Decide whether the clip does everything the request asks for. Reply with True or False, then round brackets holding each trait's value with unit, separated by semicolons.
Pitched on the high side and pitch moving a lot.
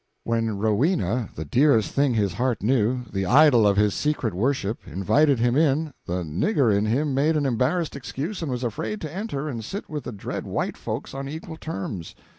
False (125 Hz; 5.9 semitones)